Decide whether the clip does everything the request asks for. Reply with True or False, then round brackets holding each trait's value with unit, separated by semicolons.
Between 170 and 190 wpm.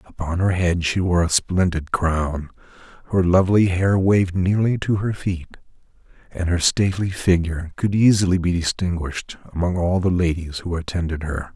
False (160 wpm)